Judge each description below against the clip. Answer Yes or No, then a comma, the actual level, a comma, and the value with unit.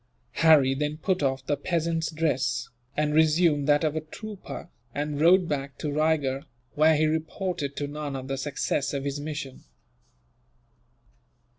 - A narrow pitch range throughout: Yes, narrow, 2.2 semitones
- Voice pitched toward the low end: No, medium, 150 Hz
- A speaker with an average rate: Yes, average, 145 wpm